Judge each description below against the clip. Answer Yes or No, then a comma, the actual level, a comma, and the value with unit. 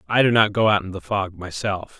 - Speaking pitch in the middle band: No, low, 100 Hz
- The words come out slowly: No, fast, 270 wpm